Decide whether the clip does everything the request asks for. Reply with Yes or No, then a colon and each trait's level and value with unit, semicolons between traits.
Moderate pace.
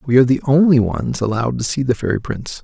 No: fast, 250 wpm